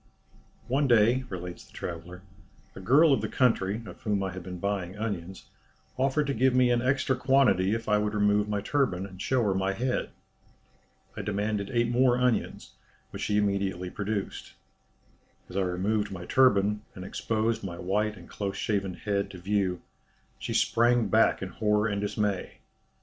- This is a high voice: No, low, 105 Hz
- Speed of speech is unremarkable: Yes, average, 170 wpm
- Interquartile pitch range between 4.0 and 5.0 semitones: No, average, 3.6 semitones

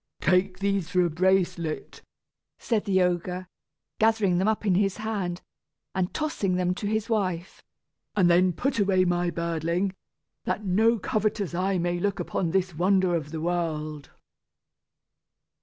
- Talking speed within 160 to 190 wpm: No, average, 145 wpm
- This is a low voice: No, medium, 185 Hz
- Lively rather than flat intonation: No, narrow, 2.4 semitones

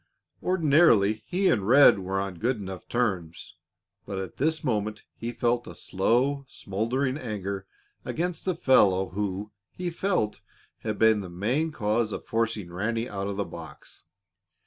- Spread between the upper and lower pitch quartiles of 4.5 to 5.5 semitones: Yes, average, 5.2 semitones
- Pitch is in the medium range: No, low, 110 Hz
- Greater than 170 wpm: No, average, 150 wpm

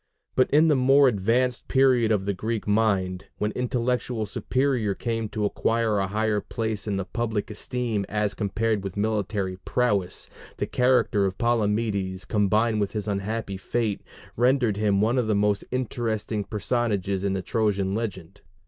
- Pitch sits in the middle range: No, low, 110 Hz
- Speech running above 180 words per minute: No, average, 155 wpm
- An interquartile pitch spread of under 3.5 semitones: Yes, average, 2.8 semitones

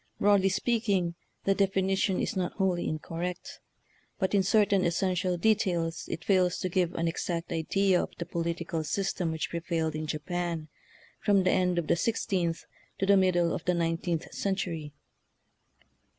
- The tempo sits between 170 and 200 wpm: No, average, 160 wpm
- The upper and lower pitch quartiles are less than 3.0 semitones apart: Yes, narrow, 2.5 semitones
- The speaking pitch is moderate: Yes, medium, 180 Hz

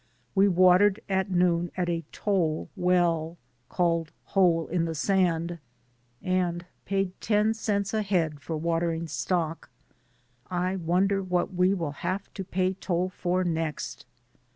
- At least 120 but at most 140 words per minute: Yes, slow, 135 wpm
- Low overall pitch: No, medium, 180 Hz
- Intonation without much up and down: Yes, narrow, 2.3 semitones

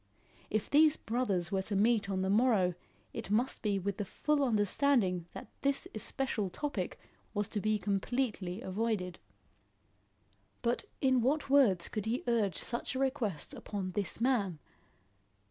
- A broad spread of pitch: No, average, 4.6 semitones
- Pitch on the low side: No, high, 215 Hz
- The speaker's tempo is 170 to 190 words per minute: No, average, 145 wpm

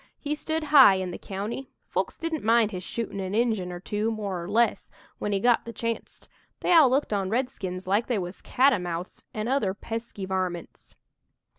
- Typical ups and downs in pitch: Yes, average, 4.5 semitones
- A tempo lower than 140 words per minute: No, average, 185 wpm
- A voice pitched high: Yes, high, 215 Hz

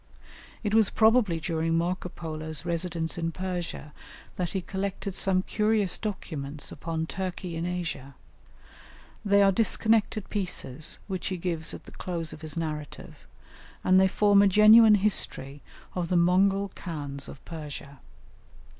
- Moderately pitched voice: Yes, medium, 180 Hz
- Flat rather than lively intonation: No, average, 3.6 semitones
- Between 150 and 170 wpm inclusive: No, average, 140 wpm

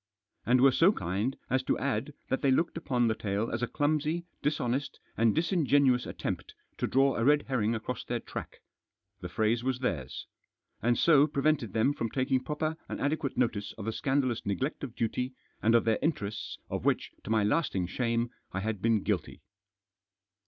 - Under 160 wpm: No, average, 185 wpm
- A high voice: No, low, 125 Hz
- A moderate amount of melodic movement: Yes, average, 4.1 semitones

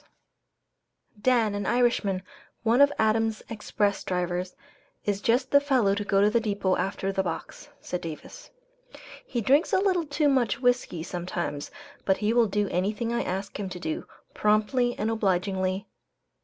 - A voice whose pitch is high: Yes, high, 210 Hz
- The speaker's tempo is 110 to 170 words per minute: Yes, average, 160 wpm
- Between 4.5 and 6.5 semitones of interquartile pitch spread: No, average, 4.1 semitones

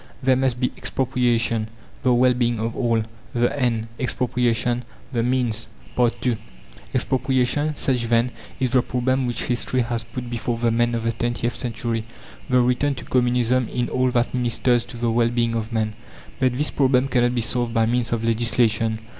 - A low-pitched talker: Yes, low, 120 Hz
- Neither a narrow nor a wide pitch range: No, narrow, 1.5 semitones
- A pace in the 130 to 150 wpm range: No, average, 175 wpm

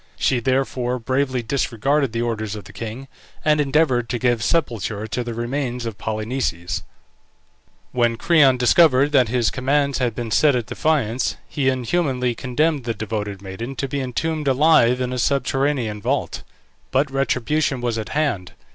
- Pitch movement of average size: Yes, average, 3.2 semitones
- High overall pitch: No, low, 125 Hz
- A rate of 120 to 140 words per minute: No, average, 155 wpm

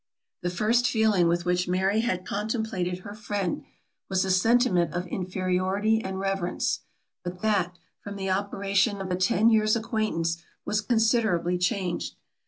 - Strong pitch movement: No, average, 3.2 semitones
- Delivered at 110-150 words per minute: Yes, average, 145 wpm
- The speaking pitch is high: Yes, high, 195 Hz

